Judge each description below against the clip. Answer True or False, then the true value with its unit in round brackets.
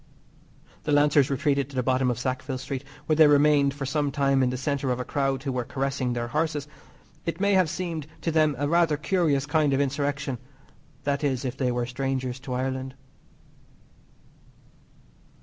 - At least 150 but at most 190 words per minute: True (180 wpm)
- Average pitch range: False (2.3 semitones)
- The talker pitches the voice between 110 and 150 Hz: True (140 Hz)